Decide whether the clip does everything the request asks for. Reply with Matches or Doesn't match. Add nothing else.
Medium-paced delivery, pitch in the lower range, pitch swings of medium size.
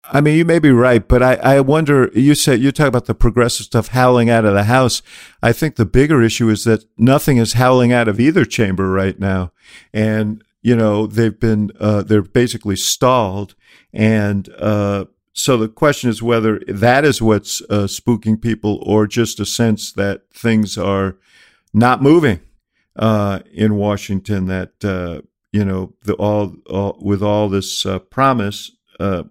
Matches